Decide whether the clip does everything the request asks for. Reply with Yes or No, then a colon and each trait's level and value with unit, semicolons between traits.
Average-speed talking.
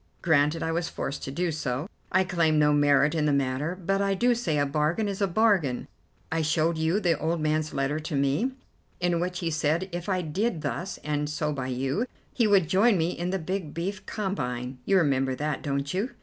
No: fast, 215 wpm